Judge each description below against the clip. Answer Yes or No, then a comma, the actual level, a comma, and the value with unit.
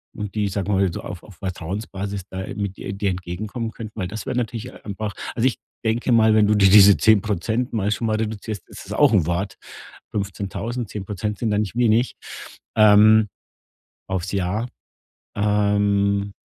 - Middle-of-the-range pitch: No, low, 105 Hz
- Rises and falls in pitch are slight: Yes, narrow, 2.0 semitones